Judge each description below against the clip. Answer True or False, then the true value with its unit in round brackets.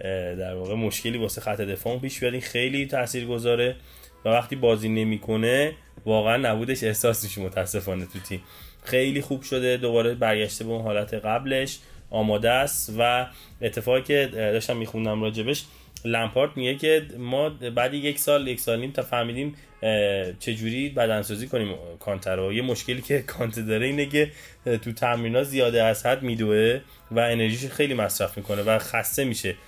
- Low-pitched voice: True (115 Hz)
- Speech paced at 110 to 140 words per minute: False (150 wpm)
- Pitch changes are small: False (3.2 semitones)